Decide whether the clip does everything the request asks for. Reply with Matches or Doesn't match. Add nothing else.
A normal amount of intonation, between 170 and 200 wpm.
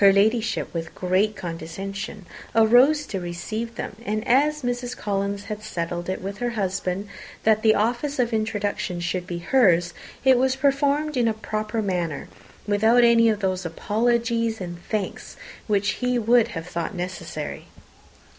Doesn't match